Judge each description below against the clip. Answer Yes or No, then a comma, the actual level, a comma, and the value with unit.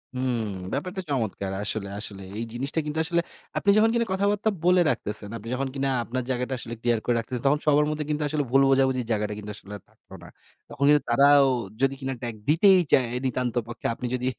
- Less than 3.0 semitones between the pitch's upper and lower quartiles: No, average, 4.2 semitones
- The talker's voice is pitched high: No, low, 130 Hz